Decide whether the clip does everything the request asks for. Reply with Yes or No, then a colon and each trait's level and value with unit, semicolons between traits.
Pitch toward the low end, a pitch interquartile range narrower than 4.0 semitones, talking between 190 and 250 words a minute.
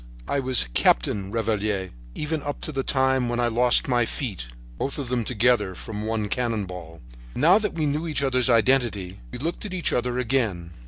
No: low, 120 Hz; average, 4.3 semitones; average, 195 wpm